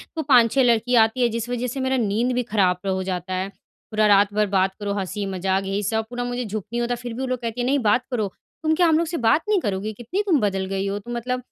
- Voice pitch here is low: No, high, 225 Hz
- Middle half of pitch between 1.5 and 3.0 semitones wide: No, average, 3.9 semitones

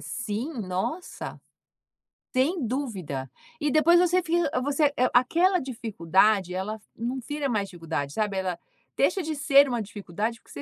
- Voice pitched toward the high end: Yes, high, 245 Hz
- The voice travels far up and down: Yes, wide, 7.3 semitones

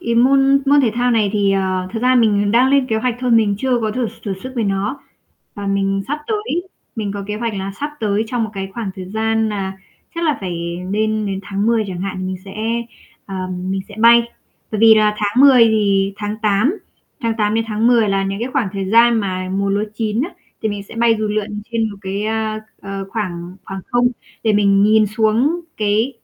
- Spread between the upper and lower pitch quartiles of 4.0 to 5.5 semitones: No, average, 2.9 semitones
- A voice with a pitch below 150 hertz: No, high, 215 Hz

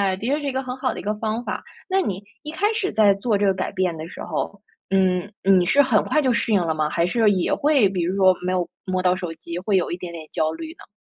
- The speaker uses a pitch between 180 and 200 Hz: Yes, high, 195 Hz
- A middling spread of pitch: Yes, average, 5.0 semitones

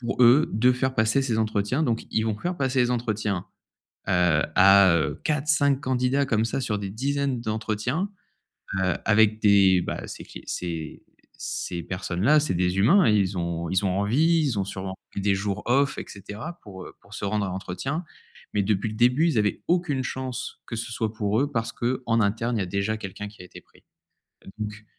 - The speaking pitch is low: Yes, low, 110 Hz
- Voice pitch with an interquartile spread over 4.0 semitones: Yes, average, 4.6 semitones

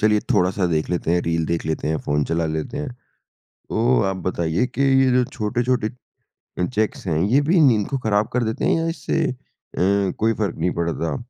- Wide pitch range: Yes, wide, 6.6 semitones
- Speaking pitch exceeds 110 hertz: No, low, 105 Hz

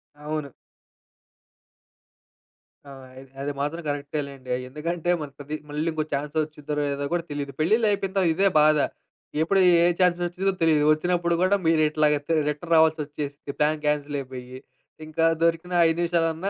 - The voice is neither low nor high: Yes, medium, 155 Hz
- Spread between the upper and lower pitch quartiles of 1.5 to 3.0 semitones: Yes, average, 2.7 semitones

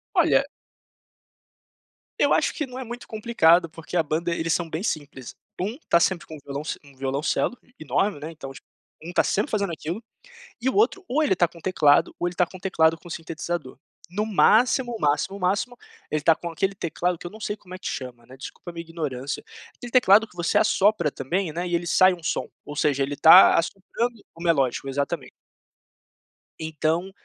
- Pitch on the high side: No, medium, 170 Hz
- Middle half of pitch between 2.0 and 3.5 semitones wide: No, average, 4.2 semitones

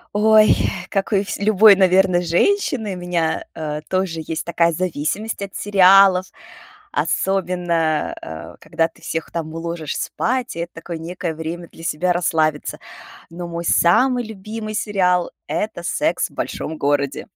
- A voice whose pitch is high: No, medium, 175 Hz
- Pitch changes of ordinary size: Yes, average, 3.2 semitones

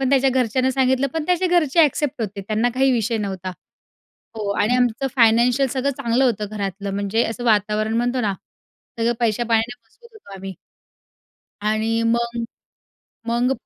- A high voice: Yes, high, 235 Hz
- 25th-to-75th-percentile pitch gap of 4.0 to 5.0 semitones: No, average, 3.5 semitones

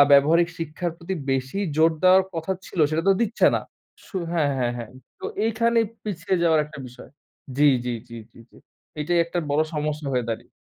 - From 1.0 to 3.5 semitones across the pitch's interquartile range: No, average, 4.4 semitones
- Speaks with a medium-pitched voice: Yes, medium, 160 Hz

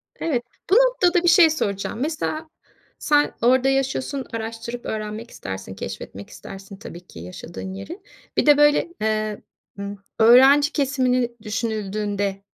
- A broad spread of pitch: Yes, wide, 6.3 semitones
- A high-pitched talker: Yes, high, 235 Hz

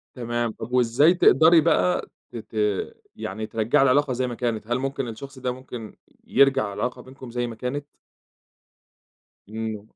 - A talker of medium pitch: No, low, 125 Hz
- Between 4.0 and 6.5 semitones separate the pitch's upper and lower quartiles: No, average, 3.2 semitones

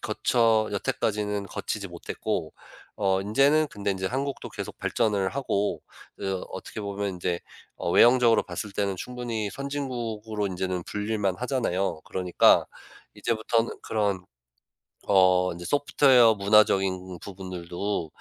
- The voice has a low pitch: Yes, low, 105 Hz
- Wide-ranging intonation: No, average, 3.5 semitones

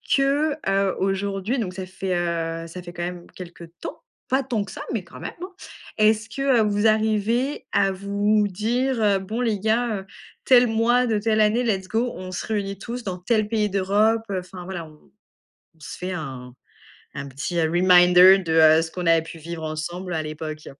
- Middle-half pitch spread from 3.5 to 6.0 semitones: Yes, average, 4.2 semitones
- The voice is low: No, high, 195 Hz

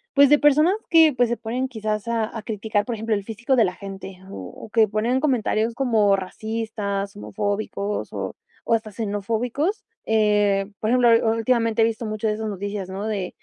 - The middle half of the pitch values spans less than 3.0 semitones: Yes, narrow, 2.5 semitones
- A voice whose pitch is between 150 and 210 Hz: No, high, 220 Hz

